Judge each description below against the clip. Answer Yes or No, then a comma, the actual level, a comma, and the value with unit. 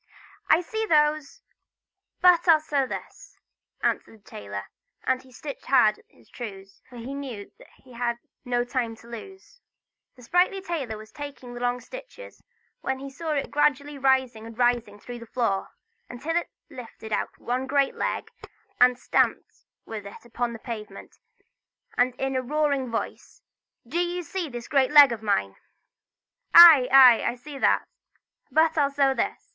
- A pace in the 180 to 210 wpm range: No, average, 165 wpm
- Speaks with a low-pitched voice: No, very high, 260 Hz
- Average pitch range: Yes, average, 4.0 semitones